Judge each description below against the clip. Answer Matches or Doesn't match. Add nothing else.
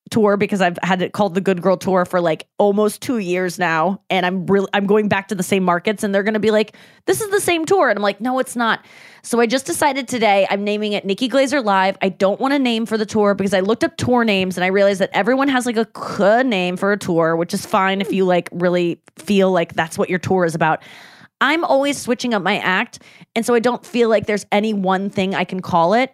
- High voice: Matches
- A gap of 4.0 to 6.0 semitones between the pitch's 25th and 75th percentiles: Doesn't match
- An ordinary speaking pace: Doesn't match